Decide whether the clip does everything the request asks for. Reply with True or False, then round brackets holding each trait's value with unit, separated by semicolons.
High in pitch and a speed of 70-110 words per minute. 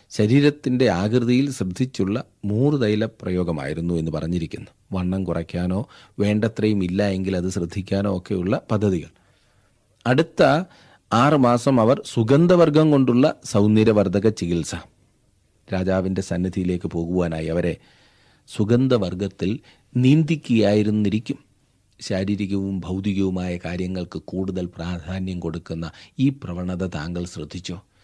False (100 Hz; 85 wpm)